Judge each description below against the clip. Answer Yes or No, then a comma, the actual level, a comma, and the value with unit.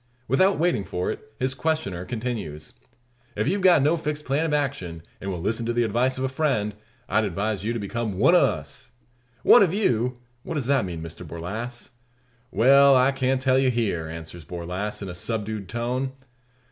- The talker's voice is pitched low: Yes, low, 120 Hz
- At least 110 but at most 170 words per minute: No, average, 190 wpm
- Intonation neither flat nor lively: No, wide, 5.9 semitones